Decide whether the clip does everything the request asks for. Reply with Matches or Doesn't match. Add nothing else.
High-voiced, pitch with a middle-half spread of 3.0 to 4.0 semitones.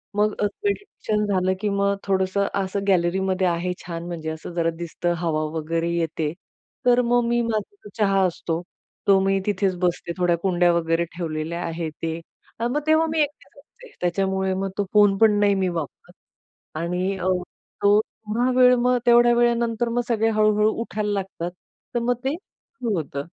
Doesn't match